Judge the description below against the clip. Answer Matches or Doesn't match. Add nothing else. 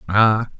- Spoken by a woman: Doesn't match